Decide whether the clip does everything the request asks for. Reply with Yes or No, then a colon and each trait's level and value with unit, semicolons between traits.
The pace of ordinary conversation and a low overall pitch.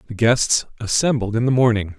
Yes: average, 180 wpm; low, 115 Hz